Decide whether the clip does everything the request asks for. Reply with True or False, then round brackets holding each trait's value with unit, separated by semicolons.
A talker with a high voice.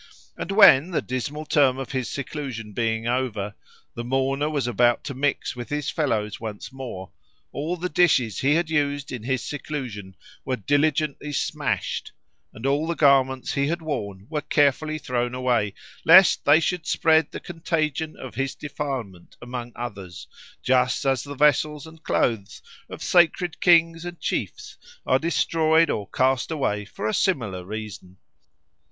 False (135 Hz)